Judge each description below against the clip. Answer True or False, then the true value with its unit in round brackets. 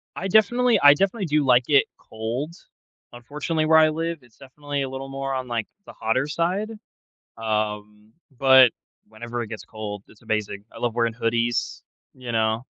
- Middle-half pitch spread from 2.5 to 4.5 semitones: False (5.0 semitones)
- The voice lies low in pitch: True (130 Hz)